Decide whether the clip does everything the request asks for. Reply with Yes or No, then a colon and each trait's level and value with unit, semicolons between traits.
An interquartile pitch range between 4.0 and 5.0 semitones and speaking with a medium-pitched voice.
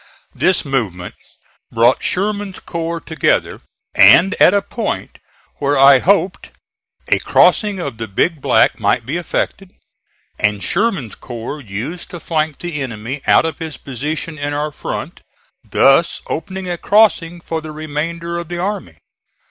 Yes: average, 4.6 semitones; medium, 155 Hz